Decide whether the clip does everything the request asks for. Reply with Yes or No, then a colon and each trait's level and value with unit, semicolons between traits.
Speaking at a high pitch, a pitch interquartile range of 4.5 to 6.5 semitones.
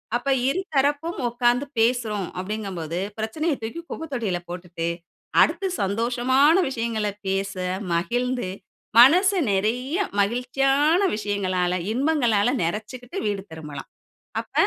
Yes: high, 235 Hz; wide, 5.5 semitones